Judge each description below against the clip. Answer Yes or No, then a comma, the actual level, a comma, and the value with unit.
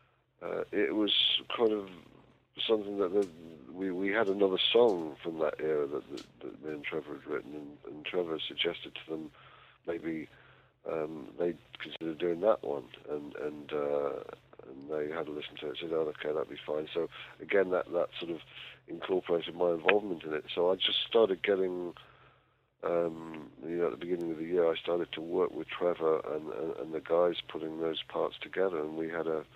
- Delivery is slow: No, average, 195 wpm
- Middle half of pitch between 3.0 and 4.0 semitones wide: Yes, average, 3.7 semitones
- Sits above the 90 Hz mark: No, very low, 85 Hz